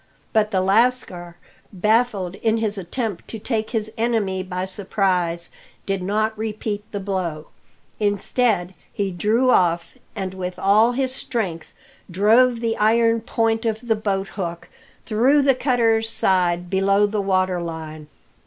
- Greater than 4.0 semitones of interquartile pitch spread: No, average, 3.4 semitones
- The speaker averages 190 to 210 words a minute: No, slow, 135 wpm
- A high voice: Yes, high, 205 Hz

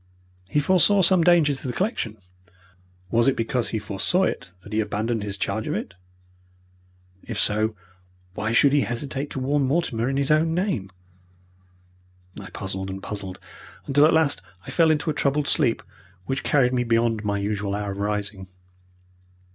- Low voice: Yes, low, 120 Hz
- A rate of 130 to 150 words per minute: No, average, 170 wpm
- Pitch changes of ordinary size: No, wide, 6.0 semitones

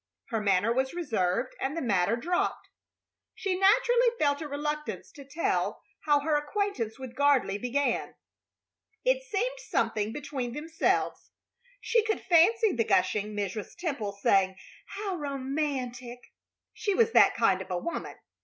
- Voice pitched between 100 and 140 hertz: No, very high, 285 Hz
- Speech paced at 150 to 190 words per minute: No, average, 140 wpm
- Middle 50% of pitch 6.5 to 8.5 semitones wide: Yes, wide, 7.5 semitones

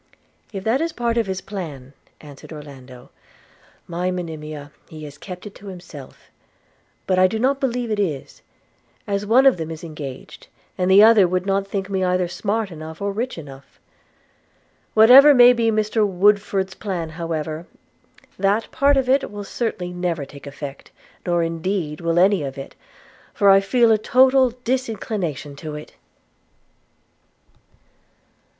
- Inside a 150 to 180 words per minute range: Yes, average, 155 wpm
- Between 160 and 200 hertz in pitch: Yes, high, 190 Hz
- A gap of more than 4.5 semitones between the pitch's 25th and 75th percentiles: Yes, wide, 5.5 semitones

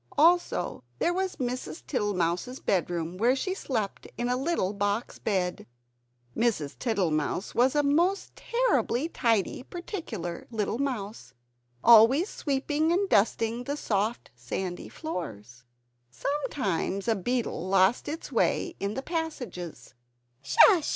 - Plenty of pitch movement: Yes, wide, 7.5 semitones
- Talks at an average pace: No, slow, 120 wpm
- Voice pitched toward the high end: Yes, high, 230 Hz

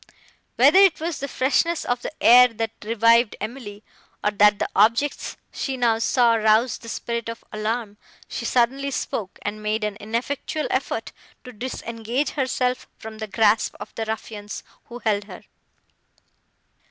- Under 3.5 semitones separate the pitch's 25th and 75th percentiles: Yes, average, 2.8 semitones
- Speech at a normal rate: Yes, average, 155 wpm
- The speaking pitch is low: No, high, 230 Hz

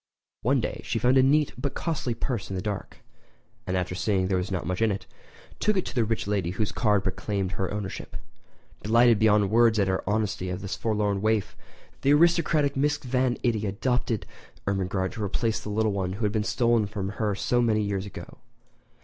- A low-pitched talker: Yes, low, 105 Hz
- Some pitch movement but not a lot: Yes, average, 3.5 semitones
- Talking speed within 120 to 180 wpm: No, fast, 205 wpm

